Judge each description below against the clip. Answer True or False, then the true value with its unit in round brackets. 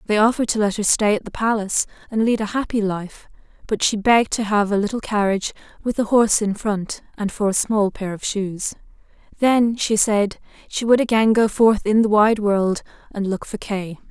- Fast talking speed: True (215 wpm)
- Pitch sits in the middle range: False (210 Hz)